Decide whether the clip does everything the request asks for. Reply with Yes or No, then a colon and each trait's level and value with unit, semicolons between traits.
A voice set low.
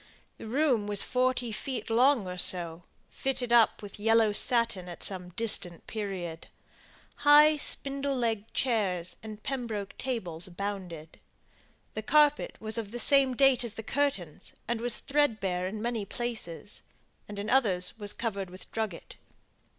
No: high, 220 Hz